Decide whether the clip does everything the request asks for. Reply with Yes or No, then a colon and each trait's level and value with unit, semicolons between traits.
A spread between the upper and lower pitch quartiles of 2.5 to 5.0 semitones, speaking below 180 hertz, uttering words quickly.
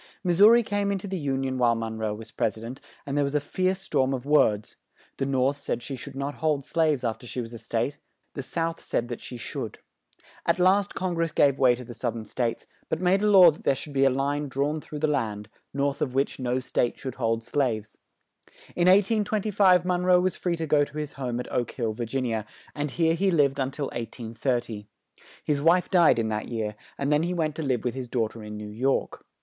No: wide, 5.6 semitones; medium, 140 Hz; fast, 245 wpm